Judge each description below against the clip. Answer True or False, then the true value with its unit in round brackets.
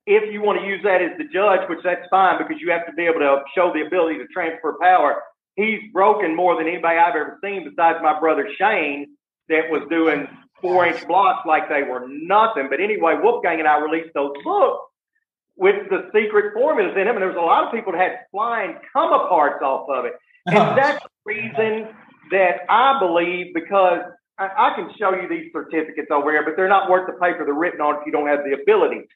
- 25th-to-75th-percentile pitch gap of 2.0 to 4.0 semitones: False (5.5 semitones)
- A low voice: False (180 Hz)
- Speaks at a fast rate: True (220 wpm)